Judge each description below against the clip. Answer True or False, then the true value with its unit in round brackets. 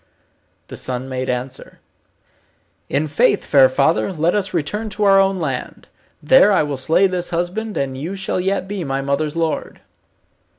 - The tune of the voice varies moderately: False (5.9 semitones)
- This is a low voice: False (165 Hz)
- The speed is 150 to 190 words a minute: True (165 wpm)